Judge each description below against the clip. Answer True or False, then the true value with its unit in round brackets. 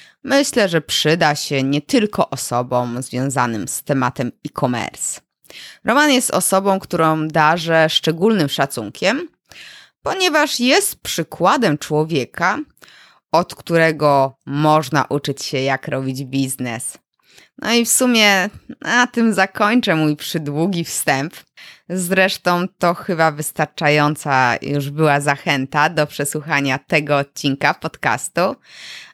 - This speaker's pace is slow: True (105 wpm)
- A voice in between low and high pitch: True (155 Hz)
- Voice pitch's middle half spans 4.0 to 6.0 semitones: True (5.1 semitones)